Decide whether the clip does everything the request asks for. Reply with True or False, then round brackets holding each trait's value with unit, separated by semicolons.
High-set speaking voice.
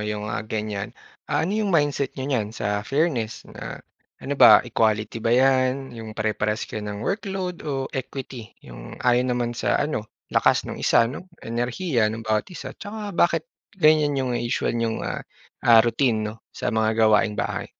False (120 Hz)